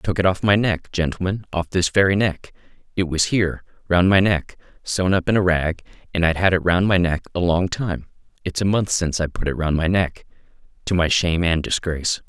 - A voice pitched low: Yes, very low, 90 Hz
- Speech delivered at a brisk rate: Yes, fast, 230 wpm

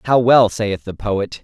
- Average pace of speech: No, fast, 210 wpm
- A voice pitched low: Yes, low, 105 Hz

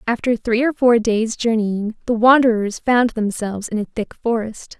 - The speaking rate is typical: Yes, average, 175 wpm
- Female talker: Yes, female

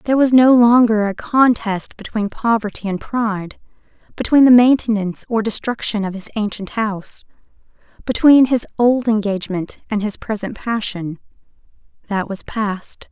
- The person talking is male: No, female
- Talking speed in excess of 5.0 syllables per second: No, 4.9 syllables/s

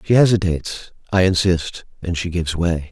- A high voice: No, very low, 90 Hz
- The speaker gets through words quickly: No, average, 165 wpm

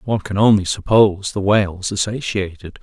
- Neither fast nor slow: Yes, average, 170 wpm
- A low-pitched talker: Yes, low, 100 Hz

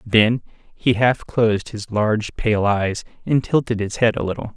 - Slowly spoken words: No, average, 185 wpm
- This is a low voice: Yes, low, 110 Hz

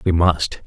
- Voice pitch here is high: No, very low, 80 Hz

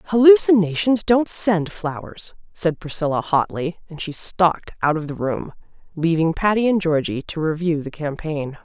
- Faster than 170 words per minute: No, average, 155 wpm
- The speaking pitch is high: No, medium, 170 Hz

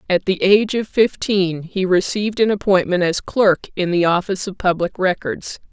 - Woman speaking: Yes, female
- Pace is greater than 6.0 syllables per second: No, 5.0 syllables/s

